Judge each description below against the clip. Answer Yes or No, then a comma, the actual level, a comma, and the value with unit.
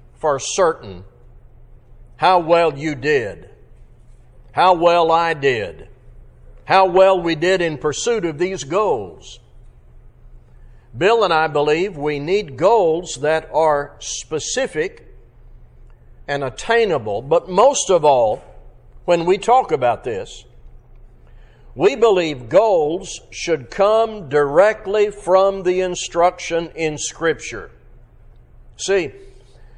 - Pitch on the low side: No, medium, 175 Hz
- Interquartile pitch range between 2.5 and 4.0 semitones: No, average, 5.1 semitones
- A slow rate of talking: Yes, slow, 105 wpm